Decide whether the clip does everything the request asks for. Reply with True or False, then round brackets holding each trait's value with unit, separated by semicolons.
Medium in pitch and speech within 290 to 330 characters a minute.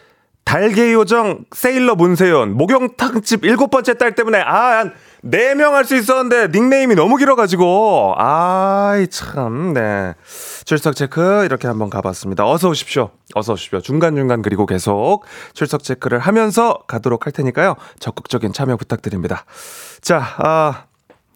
True (175 Hz; 310 characters per minute)